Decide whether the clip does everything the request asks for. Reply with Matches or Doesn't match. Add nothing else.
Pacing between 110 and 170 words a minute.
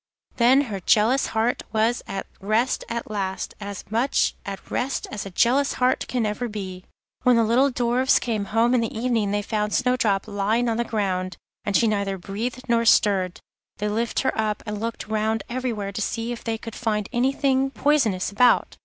Doesn't match